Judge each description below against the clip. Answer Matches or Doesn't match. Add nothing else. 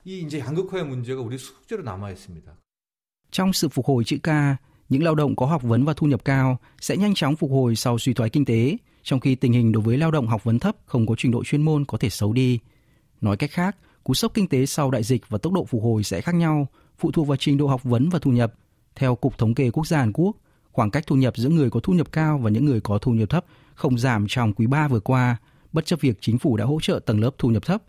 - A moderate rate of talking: Doesn't match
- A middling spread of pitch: Matches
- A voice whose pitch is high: Doesn't match